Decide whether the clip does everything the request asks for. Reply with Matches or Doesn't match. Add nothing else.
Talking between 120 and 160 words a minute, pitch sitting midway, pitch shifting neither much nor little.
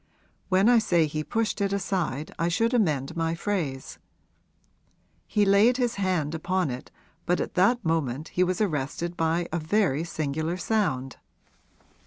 Matches